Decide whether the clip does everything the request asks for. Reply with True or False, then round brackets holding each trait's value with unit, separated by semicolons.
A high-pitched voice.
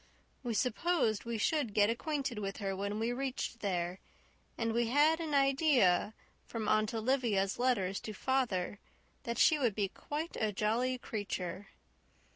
True (230 Hz)